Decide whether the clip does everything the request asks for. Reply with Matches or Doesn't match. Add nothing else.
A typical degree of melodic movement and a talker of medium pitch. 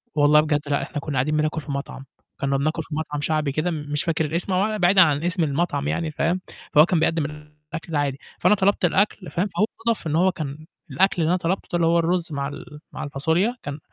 Matches